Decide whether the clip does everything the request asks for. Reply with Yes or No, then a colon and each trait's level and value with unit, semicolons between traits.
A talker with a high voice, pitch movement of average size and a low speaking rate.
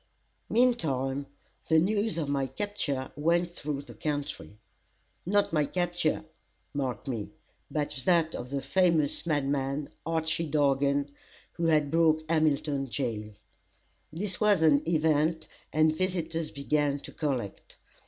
No: medium, 155 Hz; average, 3.0 semitones; slow, 125 wpm